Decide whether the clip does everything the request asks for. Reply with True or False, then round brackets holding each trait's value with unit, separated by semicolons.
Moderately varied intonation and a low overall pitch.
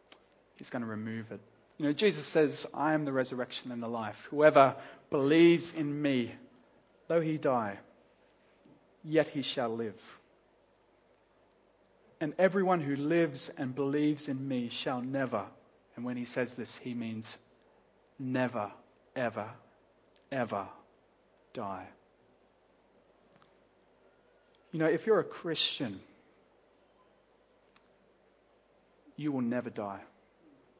True (4.3 semitones; 130 Hz)